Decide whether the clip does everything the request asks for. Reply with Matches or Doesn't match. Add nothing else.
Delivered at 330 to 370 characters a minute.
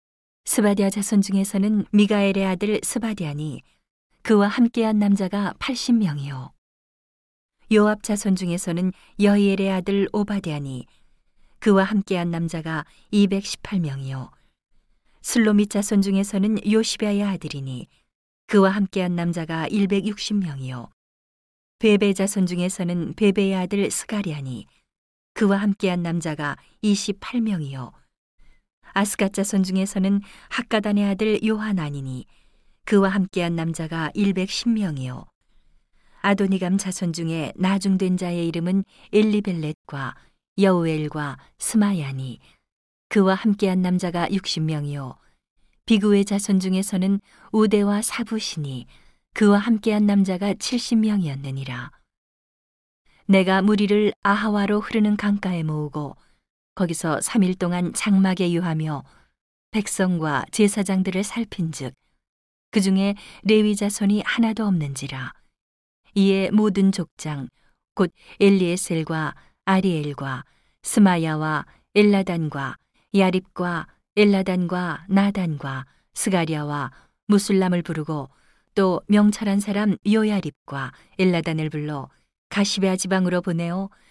Doesn't match